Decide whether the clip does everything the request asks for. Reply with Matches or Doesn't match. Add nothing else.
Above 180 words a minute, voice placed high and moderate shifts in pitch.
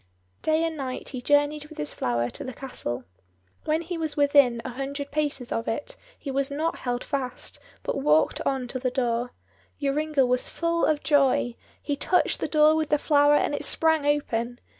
Matches